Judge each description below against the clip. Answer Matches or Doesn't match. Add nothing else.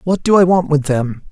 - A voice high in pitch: Doesn't match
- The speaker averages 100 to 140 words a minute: Doesn't match